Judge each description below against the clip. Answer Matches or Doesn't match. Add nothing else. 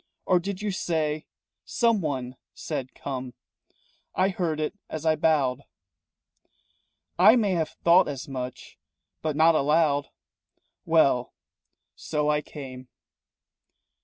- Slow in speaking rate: Matches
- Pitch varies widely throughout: Doesn't match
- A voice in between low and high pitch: Matches